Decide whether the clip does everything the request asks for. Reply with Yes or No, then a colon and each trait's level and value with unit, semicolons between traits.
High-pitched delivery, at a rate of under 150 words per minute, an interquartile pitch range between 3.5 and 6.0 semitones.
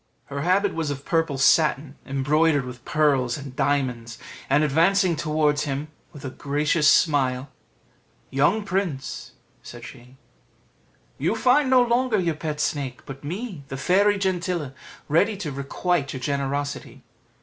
No: medium, 150 Hz; average, 140 wpm; average, 4.5 semitones